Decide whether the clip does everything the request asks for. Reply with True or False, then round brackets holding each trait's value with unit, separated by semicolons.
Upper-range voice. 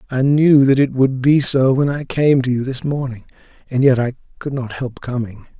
False (130 Hz)